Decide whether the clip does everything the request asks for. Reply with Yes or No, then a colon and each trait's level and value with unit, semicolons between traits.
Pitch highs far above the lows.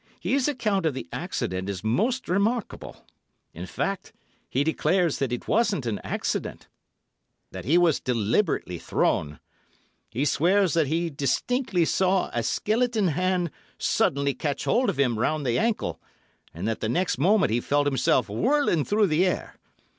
Yes: wide, 8.0 semitones